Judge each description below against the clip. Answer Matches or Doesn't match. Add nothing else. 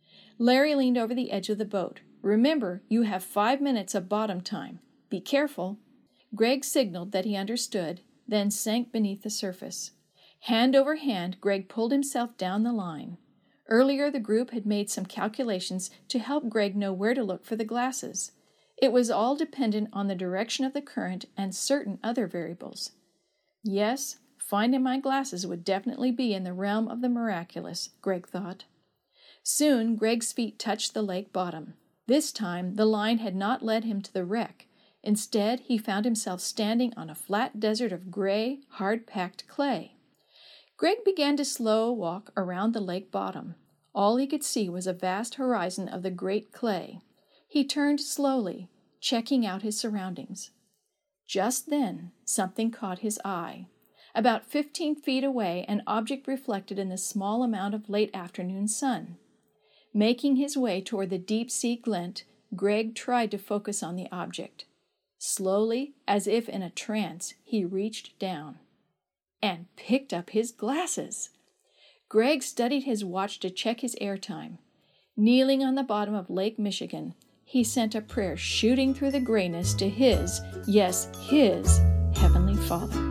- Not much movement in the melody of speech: Doesn't match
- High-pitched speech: Matches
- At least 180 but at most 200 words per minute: Doesn't match